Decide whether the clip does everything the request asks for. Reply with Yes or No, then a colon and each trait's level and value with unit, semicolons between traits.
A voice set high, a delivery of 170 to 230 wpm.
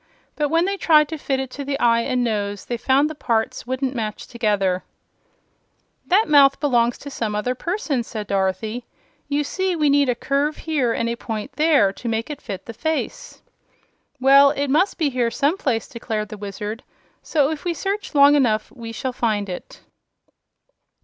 Yes: very high, 255 Hz; average, 185 wpm